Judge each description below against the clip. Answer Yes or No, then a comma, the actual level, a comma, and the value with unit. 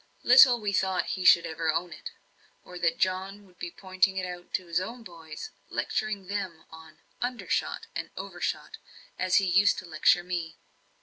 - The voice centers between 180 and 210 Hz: Yes, medium, 185 Hz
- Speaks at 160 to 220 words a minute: Yes, average, 175 wpm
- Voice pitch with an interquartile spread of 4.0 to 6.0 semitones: No, narrow, 2.6 semitones